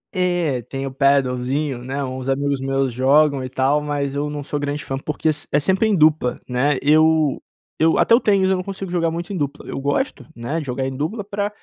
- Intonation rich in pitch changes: No, average, 3.3 semitones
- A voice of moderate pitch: Yes, medium, 145 Hz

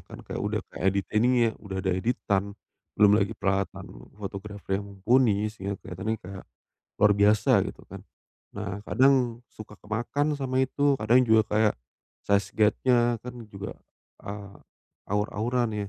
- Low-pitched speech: Yes, low, 105 Hz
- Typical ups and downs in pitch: Yes, average, 3.1 semitones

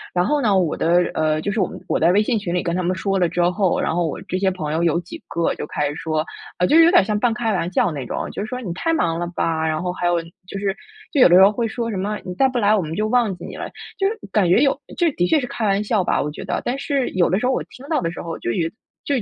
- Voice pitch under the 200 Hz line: Yes, high, 190 Hz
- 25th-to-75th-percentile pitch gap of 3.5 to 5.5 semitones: Yes, average, 5.1 semitones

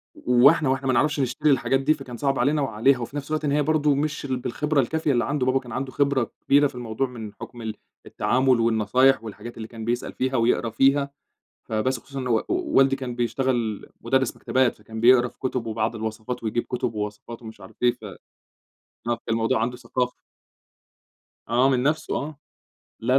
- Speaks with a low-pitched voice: Yes, low, 125 Hz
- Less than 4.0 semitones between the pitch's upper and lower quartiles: Yes, average, 2.9 semitones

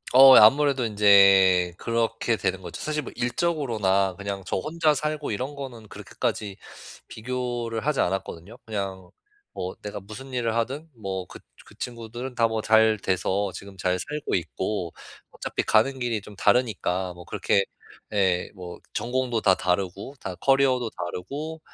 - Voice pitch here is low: Yes, low, 110 Hz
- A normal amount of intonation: Yes, average, 5.0 semitones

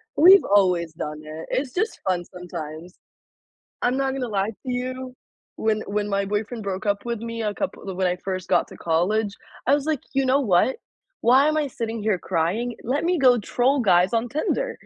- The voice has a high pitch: Yes, high, 220 Hz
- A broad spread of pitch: Yes, wide, 5.8 semitones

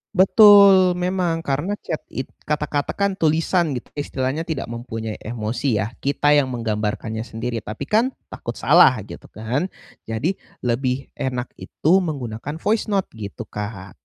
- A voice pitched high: No, low, 135 Hz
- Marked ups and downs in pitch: Yes, wide, 7.2 semitones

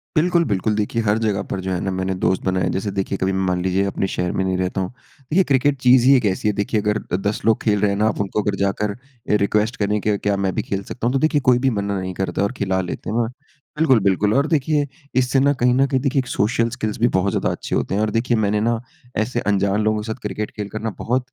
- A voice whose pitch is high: No, low, 105 Hz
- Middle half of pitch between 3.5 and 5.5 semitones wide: Yes, average, 4.0 semitones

